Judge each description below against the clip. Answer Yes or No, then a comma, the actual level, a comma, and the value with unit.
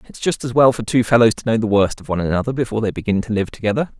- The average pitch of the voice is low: Yes, low, 115 Hz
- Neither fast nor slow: No, fast, 300 wpm